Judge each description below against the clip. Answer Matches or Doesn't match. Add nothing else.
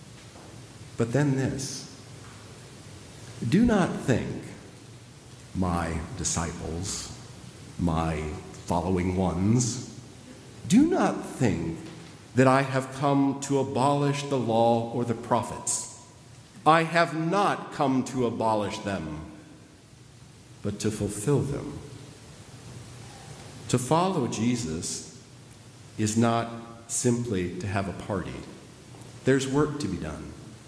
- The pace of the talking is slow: Matches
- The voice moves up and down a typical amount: Matches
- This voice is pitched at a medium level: Doesn't match